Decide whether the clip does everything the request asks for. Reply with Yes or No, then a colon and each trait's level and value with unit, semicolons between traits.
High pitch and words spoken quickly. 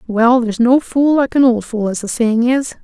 Yes: high, 240 Hz; fast, 255 wpm